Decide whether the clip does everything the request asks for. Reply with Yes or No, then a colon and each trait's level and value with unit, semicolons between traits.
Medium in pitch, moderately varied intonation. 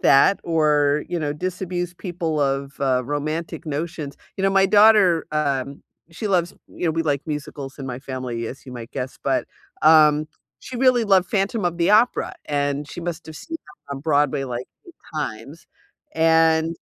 Yes: medium, 155 Hz; average, 3.9 semitones